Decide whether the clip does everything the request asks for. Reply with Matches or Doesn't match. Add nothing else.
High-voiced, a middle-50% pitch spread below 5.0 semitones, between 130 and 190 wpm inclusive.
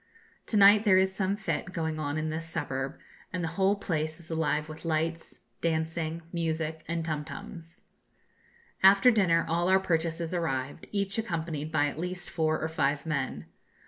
Doesn't match